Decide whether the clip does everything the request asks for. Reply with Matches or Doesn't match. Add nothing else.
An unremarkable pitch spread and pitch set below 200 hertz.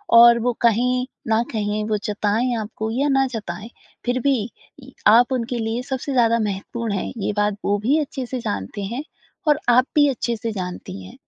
Doesn't match